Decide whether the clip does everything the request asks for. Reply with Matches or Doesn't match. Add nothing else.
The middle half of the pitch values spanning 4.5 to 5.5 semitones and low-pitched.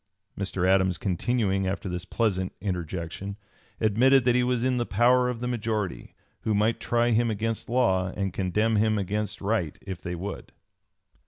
Doesn't match